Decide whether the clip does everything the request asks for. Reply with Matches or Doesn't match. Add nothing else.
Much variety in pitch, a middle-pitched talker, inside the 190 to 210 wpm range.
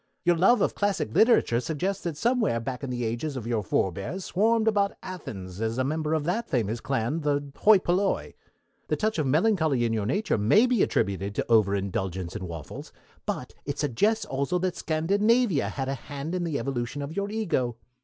Matches